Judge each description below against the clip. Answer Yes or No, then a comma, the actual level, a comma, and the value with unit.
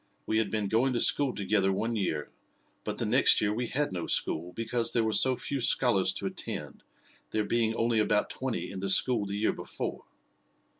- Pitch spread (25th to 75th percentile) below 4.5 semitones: Yes, average, 2.8 semitones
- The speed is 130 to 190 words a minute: No, average, 200 wpm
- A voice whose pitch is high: No, low, 110 Hz